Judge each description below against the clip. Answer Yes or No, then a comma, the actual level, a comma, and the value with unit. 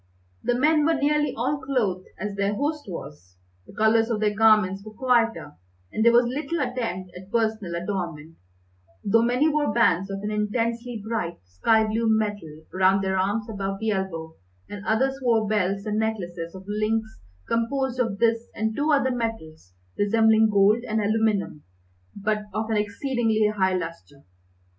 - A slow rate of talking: No, average, 160 wpm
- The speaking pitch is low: No, high, 215 Hz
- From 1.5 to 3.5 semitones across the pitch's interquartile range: Yes, average, 3.2 semitones